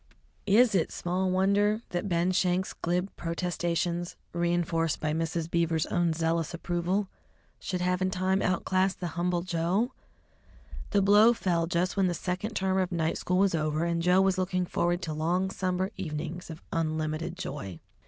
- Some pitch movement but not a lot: No, narrow, 2.0 semitones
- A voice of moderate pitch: Yes, medium, 175 Hz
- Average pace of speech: Yes, average, 165 wpm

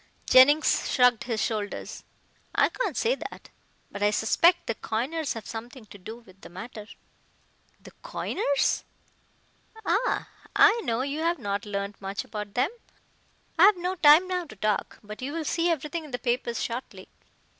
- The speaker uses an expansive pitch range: Yes, wide, 7.4 semitones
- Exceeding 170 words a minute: No, average, 165 wpm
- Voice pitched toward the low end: No, very high, 250 Hz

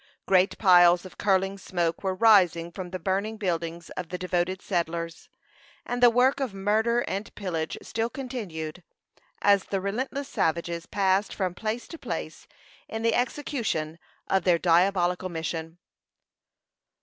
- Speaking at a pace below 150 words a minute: Yes, average, 140 wpm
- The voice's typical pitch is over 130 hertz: Yes, high, 190 Hz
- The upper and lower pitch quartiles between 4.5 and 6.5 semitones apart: No, average, 4.0 semitones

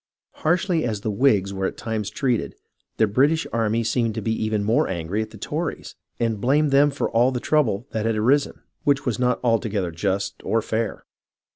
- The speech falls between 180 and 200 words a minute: Yes, average, 190 wpm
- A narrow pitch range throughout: No, average, 4.2 semitones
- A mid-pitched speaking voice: No, low, 115 Hz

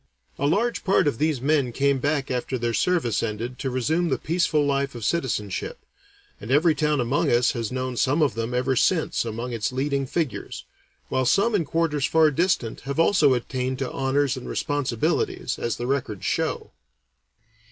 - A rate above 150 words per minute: Yes, average, 175 wpm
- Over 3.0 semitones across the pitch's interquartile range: Yes, average, 3.9 semitones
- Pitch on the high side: No, low, 135 Hz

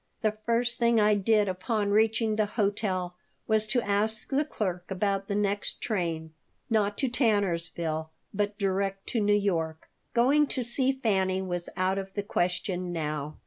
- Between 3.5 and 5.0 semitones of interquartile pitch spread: No, average, 3.1 semitones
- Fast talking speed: No, average, 160 wpm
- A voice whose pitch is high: Yes, high, 205 Hz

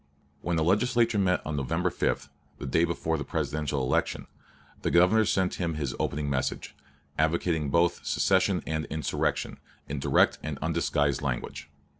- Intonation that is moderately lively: Yes, average, 3.3 semitones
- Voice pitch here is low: Yes, very low, 80 Hz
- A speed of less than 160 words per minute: Yes, average, 150 wpm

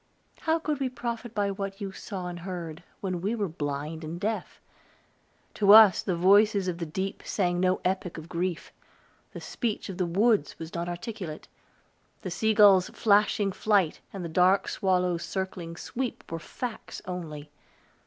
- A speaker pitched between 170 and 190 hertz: Yes, medium, 185 Hz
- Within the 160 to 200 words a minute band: Yes, average, 165 wpm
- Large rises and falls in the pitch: No, average, 3.3 semitones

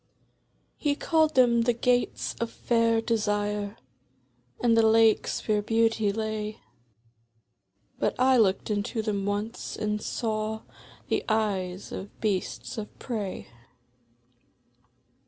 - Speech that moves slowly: Yes, slow, 110 wpm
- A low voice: No, high, 220 Hz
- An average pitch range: No, narrow, 1.9 semitones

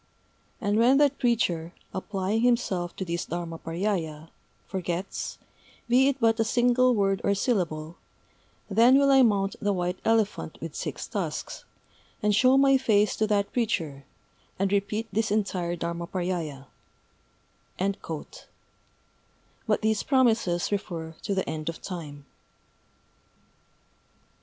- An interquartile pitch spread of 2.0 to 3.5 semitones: No, average, 4.7 semitones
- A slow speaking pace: Yes, slow, 120 wpm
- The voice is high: Yes, high, 200 Hz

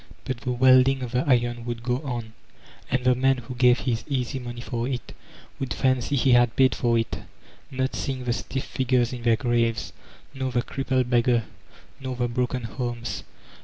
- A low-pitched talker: Yes, low, 125 Hz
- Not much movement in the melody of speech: Yes, narrow, 1.5 semitones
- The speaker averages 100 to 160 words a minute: No, average, 190 wpm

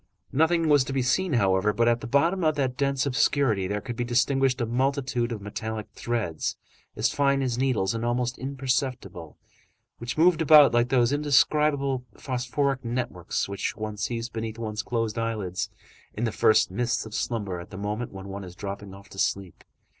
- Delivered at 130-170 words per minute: No, average, 185 wpm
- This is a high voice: No, low, 120 Hz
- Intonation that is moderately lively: Yes, average, 4.3 semitones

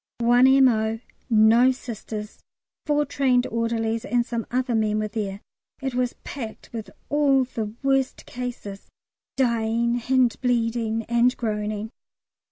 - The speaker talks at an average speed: No, slow, 125 wpm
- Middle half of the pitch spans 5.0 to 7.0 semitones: No, narrow, 2.4 semitones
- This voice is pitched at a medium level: No, high, 235 Hz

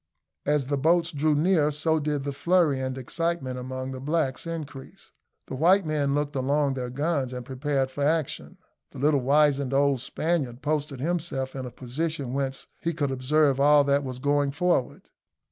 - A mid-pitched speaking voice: Yes, medium, 145 Hz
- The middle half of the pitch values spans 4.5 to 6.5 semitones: No, average, 2.7 semitones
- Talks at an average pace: Yes, average, 175 wpm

